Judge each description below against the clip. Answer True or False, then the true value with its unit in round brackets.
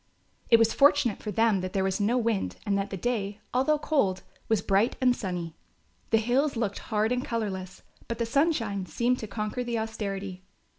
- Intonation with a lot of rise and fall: False (3.6 semitones)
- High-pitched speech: True (220 Hz)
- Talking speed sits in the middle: True (190 wpm)